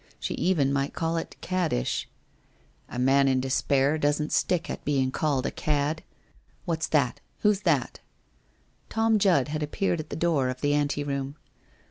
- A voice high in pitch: No, medium, 145 Hz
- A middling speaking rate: Yes, average, 165 wpm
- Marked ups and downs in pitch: No, average, 3.1 semitones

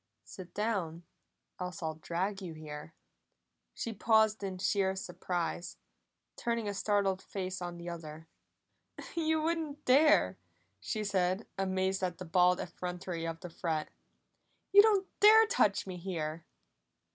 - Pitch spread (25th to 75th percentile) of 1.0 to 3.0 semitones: No, average, 3.9 semitones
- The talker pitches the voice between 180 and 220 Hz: Yes, medium, 185 Hz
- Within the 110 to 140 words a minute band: Yes, slow, 135 wpm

